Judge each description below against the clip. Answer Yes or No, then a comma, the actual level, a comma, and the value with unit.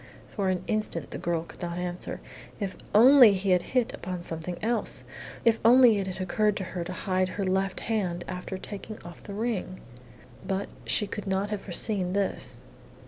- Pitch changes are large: No, average, 2.8 semitones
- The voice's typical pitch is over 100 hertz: Yes, high, 190 Hz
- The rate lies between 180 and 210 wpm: Yes, average, 185 wpm